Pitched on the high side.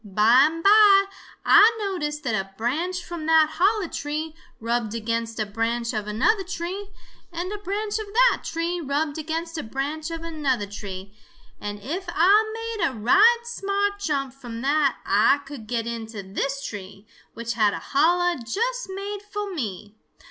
Yes: very high, 305 Hz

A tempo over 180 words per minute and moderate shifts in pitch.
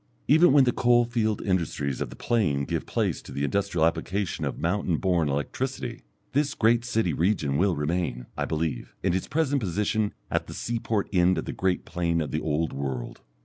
No: average, 190 wpm; wide, 6.2 semitones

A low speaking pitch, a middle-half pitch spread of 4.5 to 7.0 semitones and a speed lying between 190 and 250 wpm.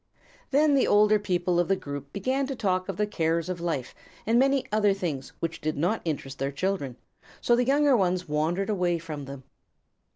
No: medium, 185 Hz; average, 5.3 semitones; average, 195 wpm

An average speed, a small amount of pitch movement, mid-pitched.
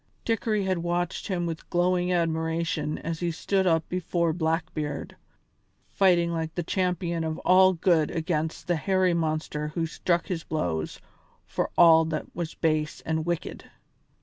Yes: average, 150 wpm; narrow, 1.9 semitones; medium, 170 Hz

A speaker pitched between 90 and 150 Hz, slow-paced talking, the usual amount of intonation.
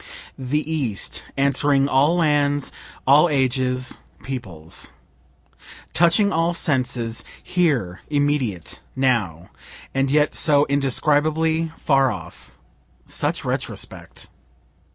Yes: medium, 140 Hz; slow, 90 wpm; average, 3.1 semitones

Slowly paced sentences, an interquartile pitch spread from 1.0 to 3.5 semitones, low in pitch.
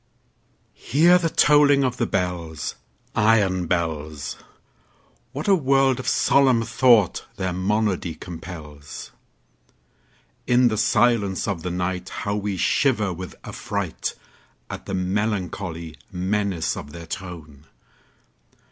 No: slow, 95 wpm; wide, 5.5 semitones; very low, 95 Hz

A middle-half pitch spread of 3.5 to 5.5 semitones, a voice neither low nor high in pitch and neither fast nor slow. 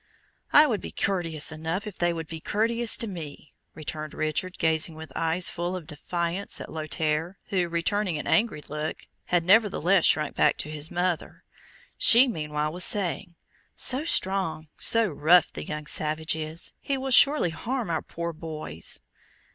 Yes: average, 4.0 semitones; medium, 170 Hz; average, 165 wpm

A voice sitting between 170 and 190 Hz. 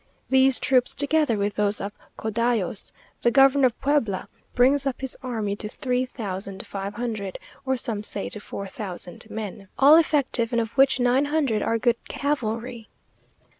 No: high, 235 Hz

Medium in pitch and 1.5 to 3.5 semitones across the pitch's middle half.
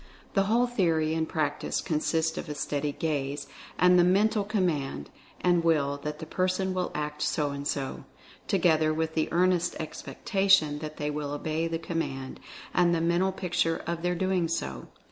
Yes: medium, 165 Hz; average, 3.2 semitones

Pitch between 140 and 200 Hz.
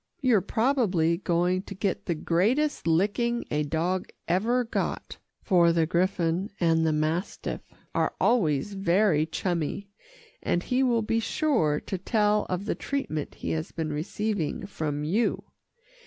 Yes: medium, 185 Hz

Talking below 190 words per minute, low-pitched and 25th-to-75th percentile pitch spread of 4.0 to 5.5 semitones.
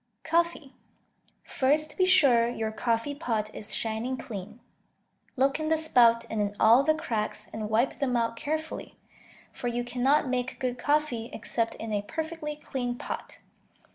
No: average, 155 wpm; high, 245 Hz; average, 4.8 semitones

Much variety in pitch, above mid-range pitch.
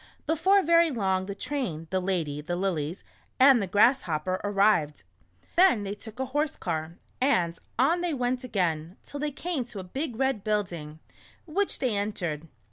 Yes: wide, 7.5 semitones; high, 205 Hz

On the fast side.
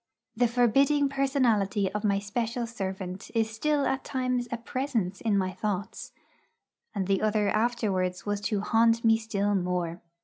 No: average, 150 wpm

